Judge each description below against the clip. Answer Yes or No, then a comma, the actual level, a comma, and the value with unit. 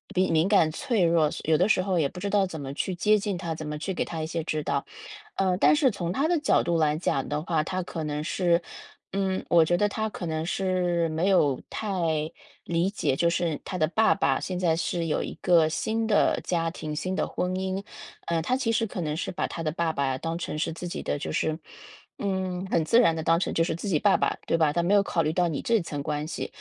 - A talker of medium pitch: Yes, medium, 170 Hz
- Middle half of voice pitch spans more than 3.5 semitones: No, average, 3.2 semitones